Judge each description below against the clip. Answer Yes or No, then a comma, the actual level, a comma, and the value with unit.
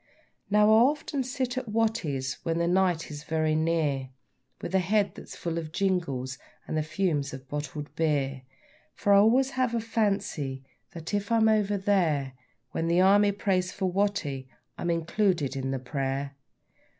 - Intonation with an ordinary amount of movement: No, wide, 5.9 semitones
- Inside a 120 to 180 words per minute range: Yes, average, 170 wpm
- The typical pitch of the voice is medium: Yes, medium, 170 Hz